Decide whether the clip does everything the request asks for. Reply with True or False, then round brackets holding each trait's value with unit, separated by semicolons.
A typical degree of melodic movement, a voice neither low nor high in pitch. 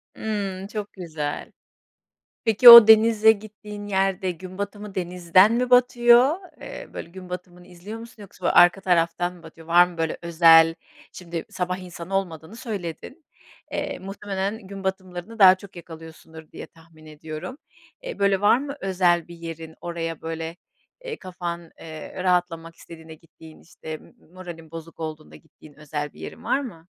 True (3.7 semitones; 180 Hz)